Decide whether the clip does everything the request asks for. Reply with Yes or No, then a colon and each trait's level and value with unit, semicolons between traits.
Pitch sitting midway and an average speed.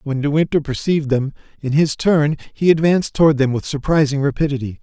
Yes: medium, 145 Hz; average, 185 wpm